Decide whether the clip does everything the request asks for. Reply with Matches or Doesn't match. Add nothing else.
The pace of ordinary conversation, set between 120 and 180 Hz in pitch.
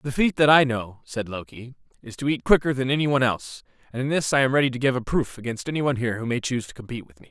Doesn't match